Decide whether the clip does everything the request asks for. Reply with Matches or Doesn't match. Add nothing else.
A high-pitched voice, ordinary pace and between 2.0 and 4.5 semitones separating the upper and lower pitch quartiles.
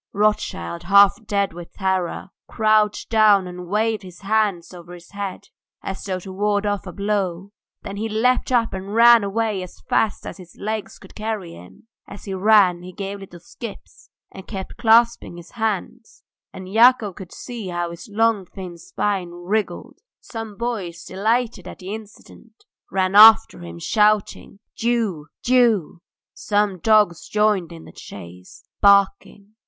Matches